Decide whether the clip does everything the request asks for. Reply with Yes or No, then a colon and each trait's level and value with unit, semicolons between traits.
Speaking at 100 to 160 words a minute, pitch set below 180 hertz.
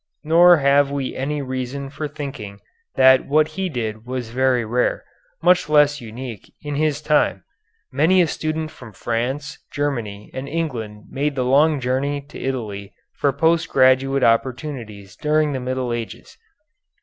Yes: average, 150 wpm; low, 135 Hz